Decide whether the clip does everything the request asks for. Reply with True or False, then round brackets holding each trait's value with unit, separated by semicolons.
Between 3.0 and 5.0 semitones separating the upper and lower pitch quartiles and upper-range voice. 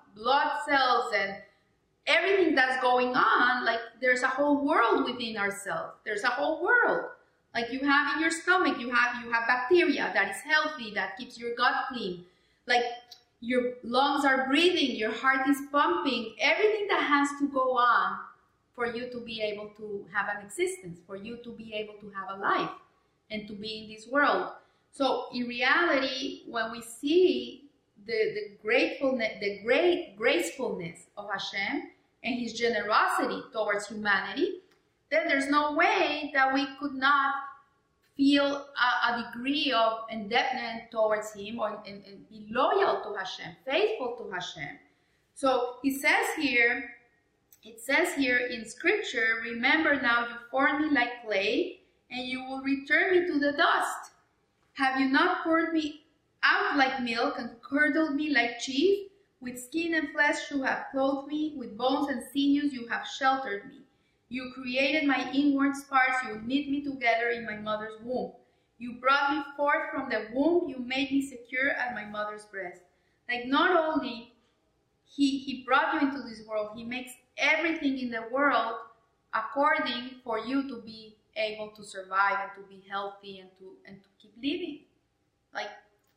True (4.3 semitones; 260 Hz)